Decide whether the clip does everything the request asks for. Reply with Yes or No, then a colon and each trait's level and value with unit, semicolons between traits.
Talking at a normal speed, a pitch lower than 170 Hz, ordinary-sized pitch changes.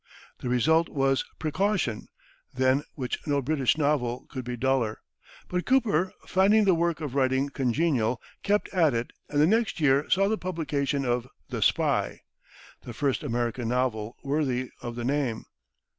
Yes: average, 155 wpm; medium, 140 Hz; average, 4.7 semitones